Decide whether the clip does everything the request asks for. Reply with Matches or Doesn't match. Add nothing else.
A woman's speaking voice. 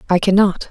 Matches